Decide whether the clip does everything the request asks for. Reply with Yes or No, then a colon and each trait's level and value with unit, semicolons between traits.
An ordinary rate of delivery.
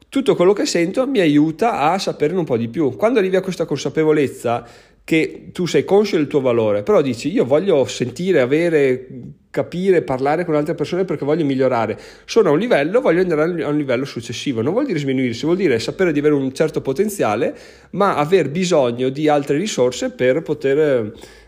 No: fast, 190 wpm